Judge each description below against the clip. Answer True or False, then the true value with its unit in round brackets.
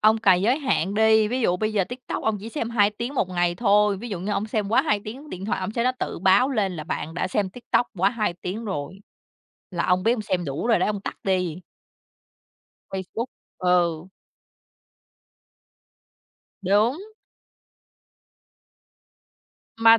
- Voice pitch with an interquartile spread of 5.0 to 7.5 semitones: False (3.6 semitones)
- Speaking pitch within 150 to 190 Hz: False (205 Hz)